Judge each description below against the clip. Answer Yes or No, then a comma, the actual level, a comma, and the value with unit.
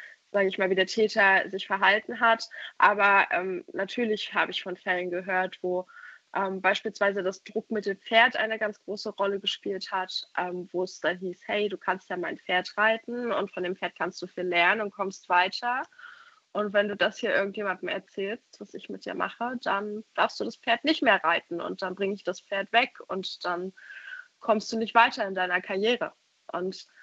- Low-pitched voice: No, high, 195 Hz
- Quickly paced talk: Yes, fast, 200 wpm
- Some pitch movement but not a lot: Yes, average, 3.0 semitones